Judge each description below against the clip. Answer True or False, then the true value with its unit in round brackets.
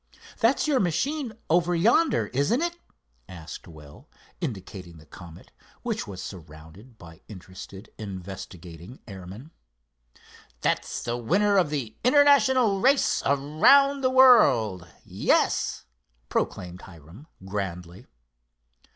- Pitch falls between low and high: False (120 Hz)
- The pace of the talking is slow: True (105 wpm)